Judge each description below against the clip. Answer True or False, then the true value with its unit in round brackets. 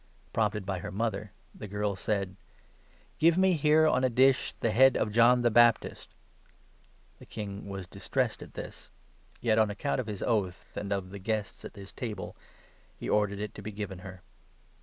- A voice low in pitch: True (105 Hz)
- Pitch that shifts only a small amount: False (3.1 semitones)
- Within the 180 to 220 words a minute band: True (185 wpm)